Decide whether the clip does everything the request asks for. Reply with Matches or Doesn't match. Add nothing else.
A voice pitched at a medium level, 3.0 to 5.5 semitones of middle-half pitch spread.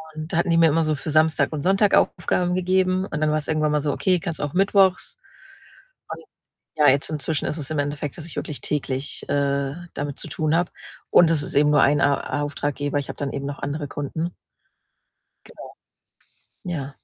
Doesn't match